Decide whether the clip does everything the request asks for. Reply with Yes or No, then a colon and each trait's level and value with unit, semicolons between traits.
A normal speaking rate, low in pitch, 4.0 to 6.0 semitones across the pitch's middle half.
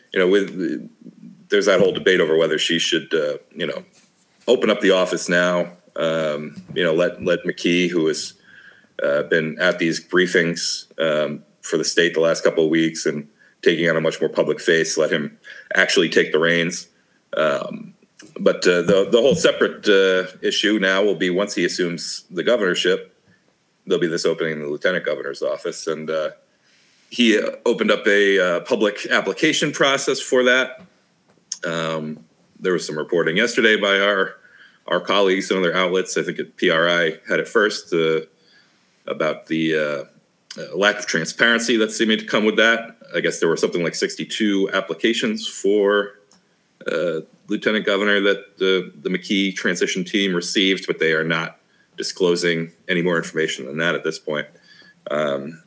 Yes: average, 170 wpm; very low, 95 Hz; average, 4.6 semitones